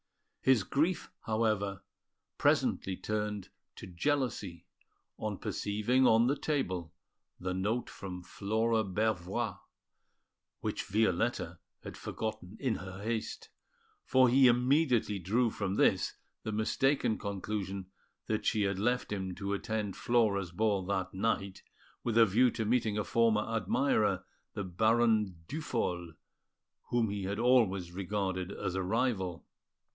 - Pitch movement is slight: No, average, 3.5 semitones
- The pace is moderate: No, slow, 125 wpm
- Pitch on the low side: Yes, low, 105 Hz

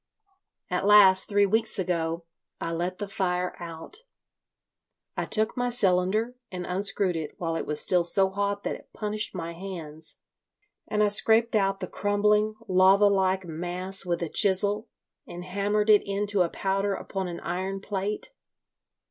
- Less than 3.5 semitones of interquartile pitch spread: Yes, narrow, 2.4 semitones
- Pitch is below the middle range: No, high, 195 Hz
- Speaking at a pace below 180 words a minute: Yes, average, 155 wpm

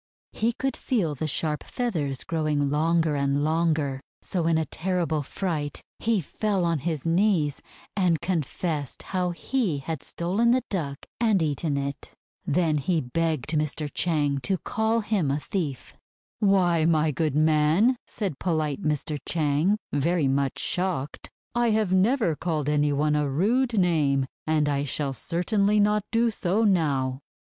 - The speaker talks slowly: No, average, 150 wpm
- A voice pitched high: No, medium, 160 Hz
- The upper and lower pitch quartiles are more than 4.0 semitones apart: Yes, average, 4.5 semitones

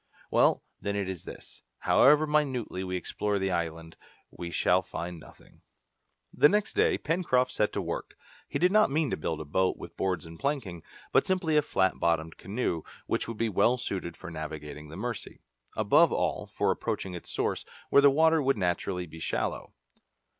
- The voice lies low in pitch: Yes, very low, 95 Hz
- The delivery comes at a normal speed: Yes, average, 180 wpm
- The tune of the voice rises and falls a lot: Yes, wide, 8.7 semitones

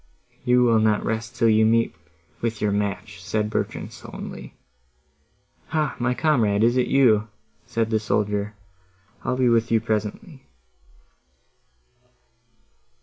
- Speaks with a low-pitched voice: Yes, low, 110 Hz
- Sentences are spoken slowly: Yes, slow, 120 wpm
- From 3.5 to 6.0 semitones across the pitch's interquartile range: No, narrow, 2.4 semitones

